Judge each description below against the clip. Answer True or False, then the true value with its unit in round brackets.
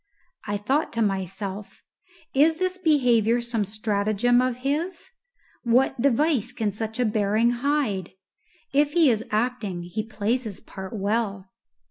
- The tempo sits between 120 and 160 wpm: True (135 wpm)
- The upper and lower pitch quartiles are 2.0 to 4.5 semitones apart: True (4.2 semitones)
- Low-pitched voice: False (230 Hz)